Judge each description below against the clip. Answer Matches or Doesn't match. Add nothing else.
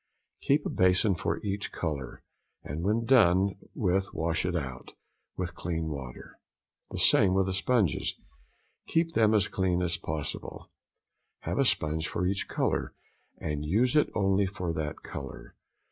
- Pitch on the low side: Matches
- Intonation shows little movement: Doesn't match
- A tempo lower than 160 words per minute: Matches